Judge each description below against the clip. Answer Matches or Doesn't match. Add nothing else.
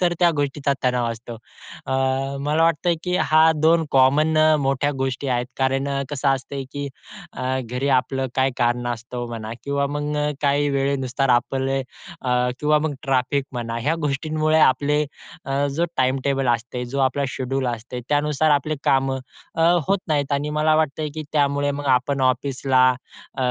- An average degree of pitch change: Doesn't match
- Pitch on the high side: Doesn't match